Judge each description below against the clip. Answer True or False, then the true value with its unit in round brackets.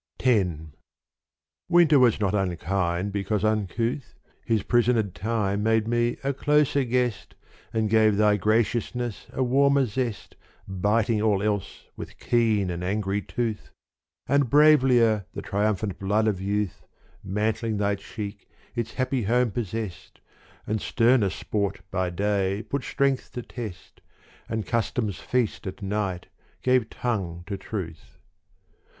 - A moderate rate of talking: False (130 wpm)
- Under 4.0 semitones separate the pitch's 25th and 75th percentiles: True (3.4 semitones)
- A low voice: True (110 Hz)